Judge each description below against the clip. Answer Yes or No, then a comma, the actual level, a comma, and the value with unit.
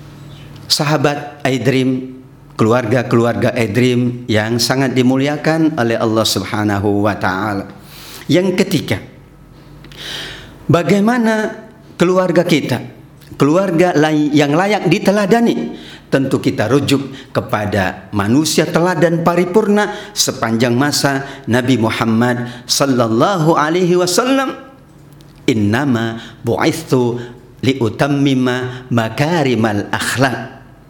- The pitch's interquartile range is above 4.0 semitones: Yes, average, 4.6 semitones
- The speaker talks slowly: Yes, slow, 80 wpm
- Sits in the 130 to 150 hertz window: Yes, low, 135 Hz